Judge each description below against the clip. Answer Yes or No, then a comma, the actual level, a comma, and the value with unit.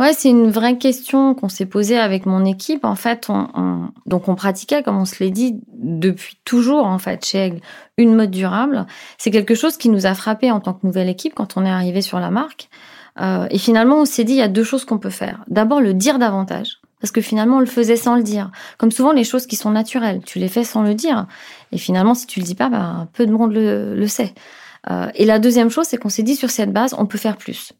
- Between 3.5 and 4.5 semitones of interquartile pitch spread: Yes, average, 4.2 semitones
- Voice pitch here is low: No, high, 220 Hz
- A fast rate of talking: Yes, fast, 260 wpm